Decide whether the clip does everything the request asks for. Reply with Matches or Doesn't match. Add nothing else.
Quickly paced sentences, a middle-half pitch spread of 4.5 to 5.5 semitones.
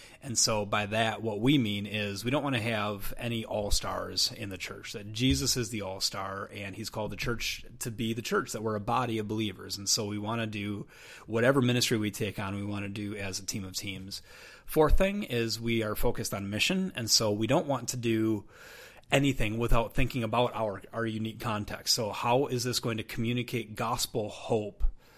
Doesn't match